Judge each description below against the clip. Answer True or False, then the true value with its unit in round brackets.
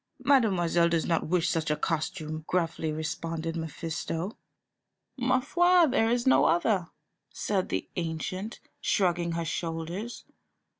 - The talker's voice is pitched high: False (170 Hz)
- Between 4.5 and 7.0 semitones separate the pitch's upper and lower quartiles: True (5.0 semitones)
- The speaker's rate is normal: False (120 wpm)